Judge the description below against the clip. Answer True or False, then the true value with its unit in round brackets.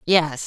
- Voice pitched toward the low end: False (160 Hz)